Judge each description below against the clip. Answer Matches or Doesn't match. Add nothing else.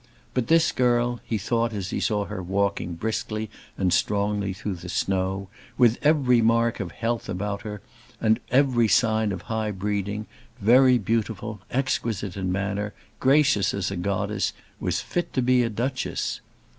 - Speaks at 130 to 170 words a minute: Matches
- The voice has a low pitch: Matches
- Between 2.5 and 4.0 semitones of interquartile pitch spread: Matches